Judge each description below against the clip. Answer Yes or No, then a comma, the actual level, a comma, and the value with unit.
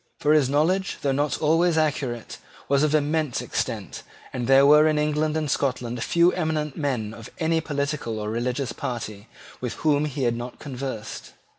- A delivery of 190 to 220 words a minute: No, average, 170 wpm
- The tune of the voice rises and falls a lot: No, average, 3.7 semitones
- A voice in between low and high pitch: Yes, medium, 145 Hz